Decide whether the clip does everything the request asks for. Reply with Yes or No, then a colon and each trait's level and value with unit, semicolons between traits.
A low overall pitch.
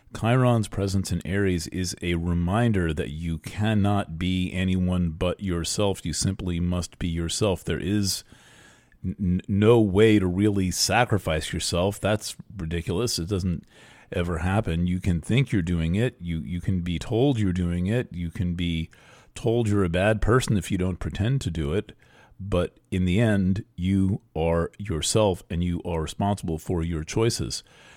Yes: very low, 95 Hz